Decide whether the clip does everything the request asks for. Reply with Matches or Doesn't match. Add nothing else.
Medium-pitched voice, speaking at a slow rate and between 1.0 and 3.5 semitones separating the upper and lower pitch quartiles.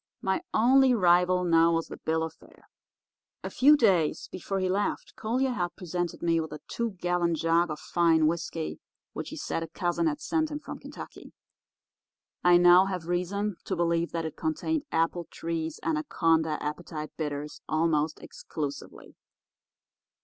Doesn't match